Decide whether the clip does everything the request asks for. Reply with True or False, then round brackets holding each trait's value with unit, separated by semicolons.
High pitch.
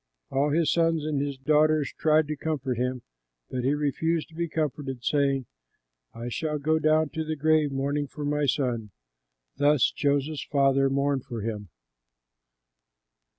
False (145 Hz)